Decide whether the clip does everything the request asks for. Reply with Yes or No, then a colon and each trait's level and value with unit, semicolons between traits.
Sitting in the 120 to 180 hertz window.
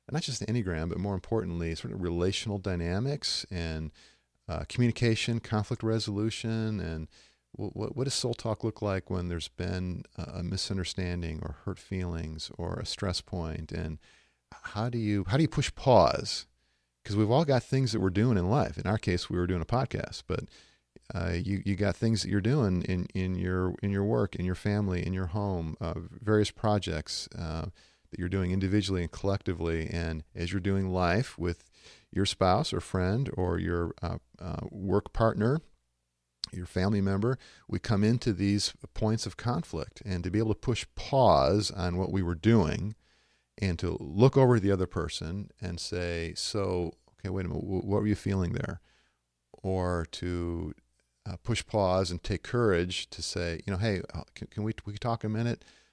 No: very low, 95 Hz